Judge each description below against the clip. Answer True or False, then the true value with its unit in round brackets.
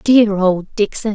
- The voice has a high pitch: True (205 Hz)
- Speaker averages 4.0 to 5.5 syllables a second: False (3.7 syllables/s)